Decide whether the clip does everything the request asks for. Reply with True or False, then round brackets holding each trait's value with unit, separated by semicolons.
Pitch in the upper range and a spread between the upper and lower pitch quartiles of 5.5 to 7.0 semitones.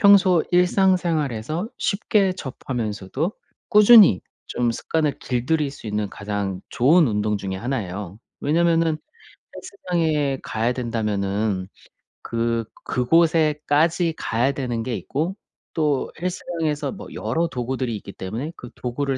False (135 Hz; 6.6 semitones)